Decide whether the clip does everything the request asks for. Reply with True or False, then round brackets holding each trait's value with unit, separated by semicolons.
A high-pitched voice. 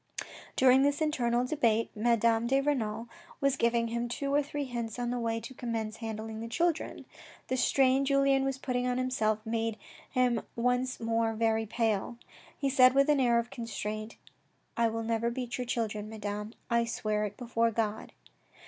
True (235 Hz)